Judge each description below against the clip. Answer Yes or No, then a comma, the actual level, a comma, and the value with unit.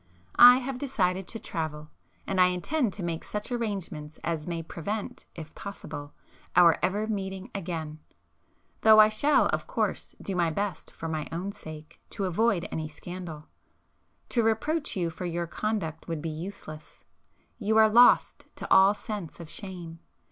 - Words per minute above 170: No, average, 160 wpm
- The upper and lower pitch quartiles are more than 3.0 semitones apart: Yes, average, 4.6 semitones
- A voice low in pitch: No, medium, 180 Hz